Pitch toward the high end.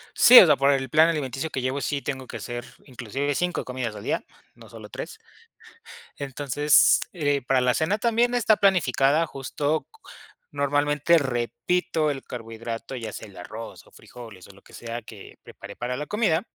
No: low, 135 Hz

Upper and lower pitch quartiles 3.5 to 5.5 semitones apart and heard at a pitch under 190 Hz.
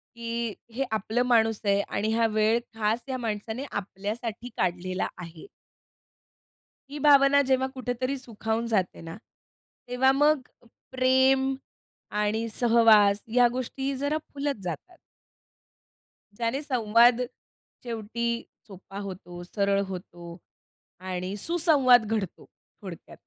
No: average, 4.2 semitones; high, 230 Hz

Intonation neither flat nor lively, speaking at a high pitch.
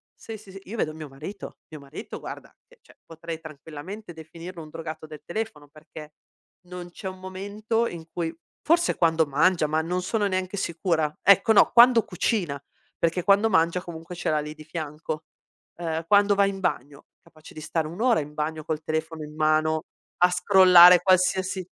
No: average, 3.4 semitones; medium, 170 Hz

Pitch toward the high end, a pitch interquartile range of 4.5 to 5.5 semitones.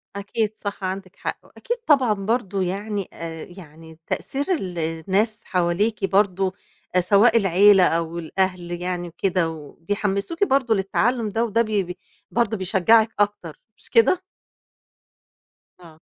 No: high, 195 Hz; average, 3.6 semitones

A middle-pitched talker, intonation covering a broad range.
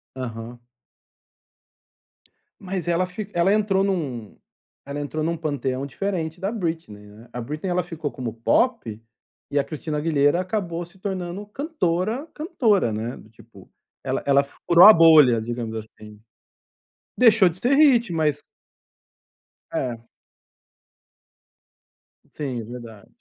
Yes: medium, 160 Hz; wide, 7.6 semitones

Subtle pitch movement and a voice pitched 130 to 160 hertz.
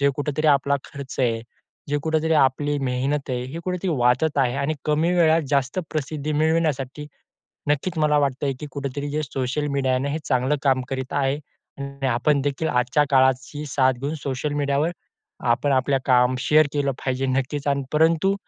Yes: narrow, 2.3 semitones; medium, 140 Hz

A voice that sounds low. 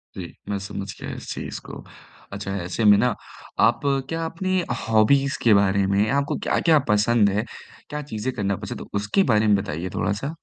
Yes: low, 105 Hz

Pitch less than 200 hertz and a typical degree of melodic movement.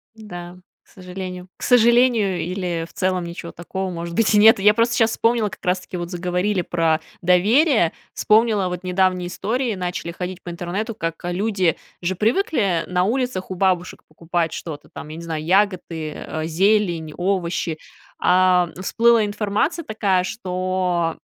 Yes: medium, 185 Hz; average, 3.3 semitones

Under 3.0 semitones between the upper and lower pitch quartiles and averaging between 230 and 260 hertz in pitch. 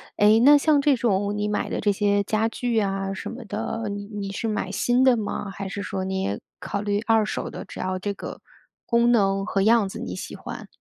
No: narrow, 2.6 semitones; high, 205 Hz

